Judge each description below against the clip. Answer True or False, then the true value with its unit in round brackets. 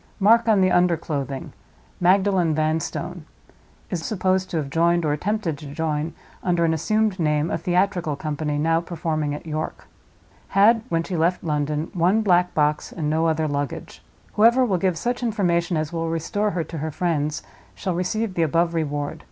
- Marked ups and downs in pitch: False (3.3 semitones)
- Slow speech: False (170 wpm)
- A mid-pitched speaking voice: True (165 Hz)